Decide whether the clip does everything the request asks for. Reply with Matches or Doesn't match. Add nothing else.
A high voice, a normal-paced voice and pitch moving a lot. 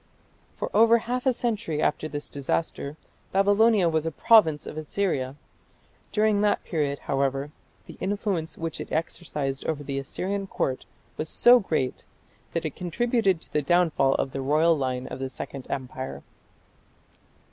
Doesn't match